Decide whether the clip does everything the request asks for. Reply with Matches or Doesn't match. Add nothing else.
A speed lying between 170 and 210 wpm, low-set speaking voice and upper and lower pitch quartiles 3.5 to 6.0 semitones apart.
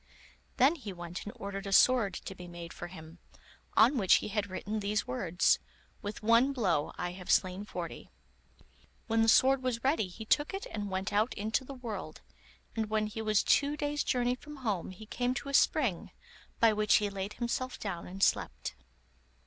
Doesn't match